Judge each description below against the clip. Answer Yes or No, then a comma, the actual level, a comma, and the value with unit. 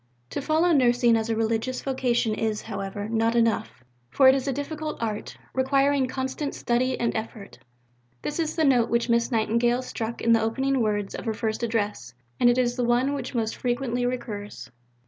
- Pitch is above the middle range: Yes, high, 240 Hz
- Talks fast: No, average, 185 wpm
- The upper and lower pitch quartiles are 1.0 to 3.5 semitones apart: Yes, average, 2.9 semitones